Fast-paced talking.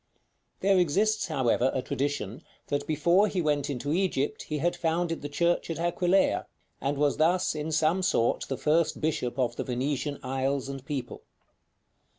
No: average, 165 wpm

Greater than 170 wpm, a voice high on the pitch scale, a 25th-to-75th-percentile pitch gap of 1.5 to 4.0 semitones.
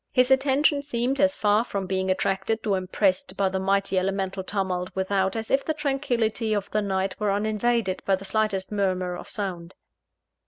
Yes: average, 180 wpm; high, 200 Hz; average, 3.3 semitones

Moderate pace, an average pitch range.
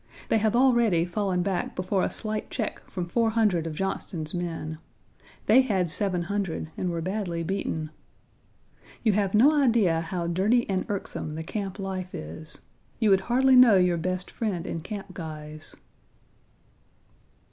Yes: average, 145 wpm; average, 4.0 semitones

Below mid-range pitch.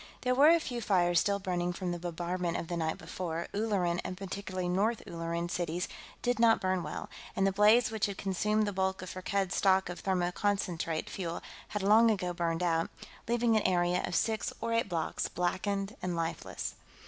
No: medium, 185 Hz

